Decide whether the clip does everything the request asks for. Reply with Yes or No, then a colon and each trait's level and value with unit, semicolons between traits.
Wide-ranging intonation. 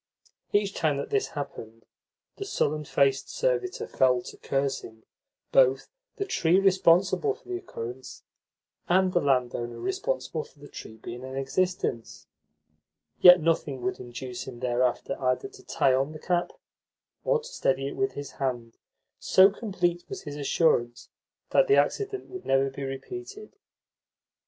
Yes: wide, 7.3 semitones